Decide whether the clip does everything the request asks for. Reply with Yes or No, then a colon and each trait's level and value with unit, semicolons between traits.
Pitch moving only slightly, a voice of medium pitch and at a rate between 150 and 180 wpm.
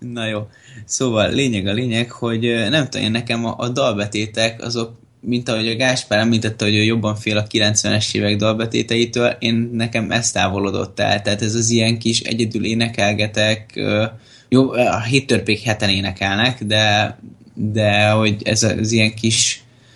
No: narrow, 1.8 semitones; low, 115 Hz; fast, 155 wpm